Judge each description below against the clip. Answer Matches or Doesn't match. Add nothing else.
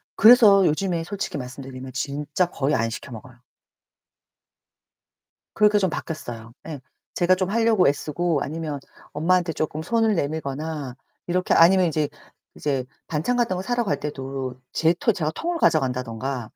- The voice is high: Doesn't match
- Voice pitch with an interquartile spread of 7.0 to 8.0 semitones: Doesn't match